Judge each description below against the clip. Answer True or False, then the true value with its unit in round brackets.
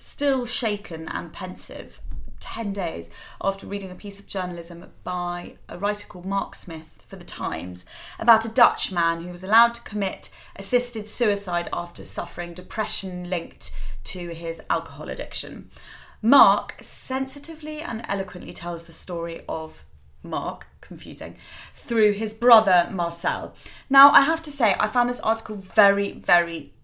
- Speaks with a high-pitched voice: True (195 Hz)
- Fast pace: False (145 wpm)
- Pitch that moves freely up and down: False (4.7 semitones)